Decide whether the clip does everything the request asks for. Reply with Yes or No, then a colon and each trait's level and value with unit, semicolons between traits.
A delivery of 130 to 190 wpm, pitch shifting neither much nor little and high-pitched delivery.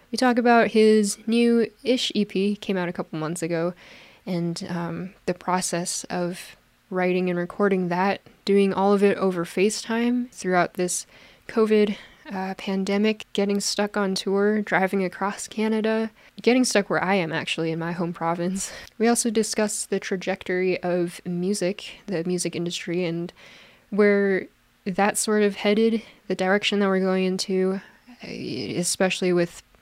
Yes: average, 150 wpm; average, 3.0 semitones; high, 195 Hz